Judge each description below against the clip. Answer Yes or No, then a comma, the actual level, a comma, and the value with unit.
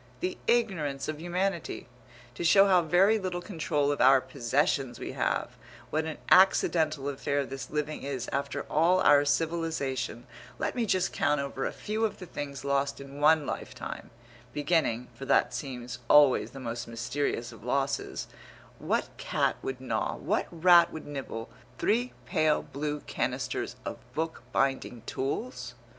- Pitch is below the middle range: No, medium, 145 Hz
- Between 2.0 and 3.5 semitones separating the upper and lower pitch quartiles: No, average, 4.0 semitones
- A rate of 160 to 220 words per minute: No, average, 150 wpm